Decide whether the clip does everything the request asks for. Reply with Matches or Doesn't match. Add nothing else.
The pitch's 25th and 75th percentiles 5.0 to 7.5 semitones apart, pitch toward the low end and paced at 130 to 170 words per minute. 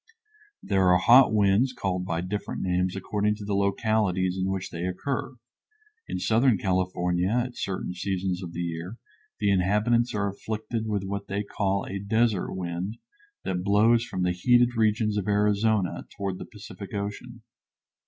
Doesn't match